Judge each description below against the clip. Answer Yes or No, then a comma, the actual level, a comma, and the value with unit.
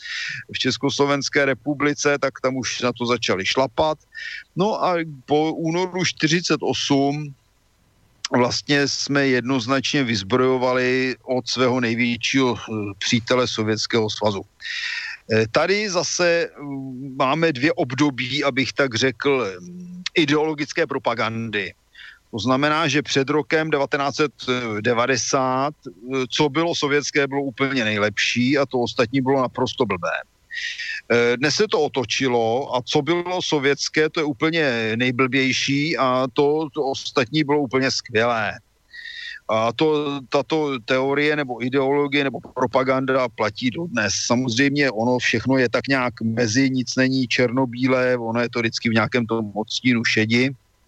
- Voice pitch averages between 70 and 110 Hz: No, low, 135 Hz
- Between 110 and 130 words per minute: Yes, average, 120 wpm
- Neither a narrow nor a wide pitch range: Yes, average, 3.3 semitones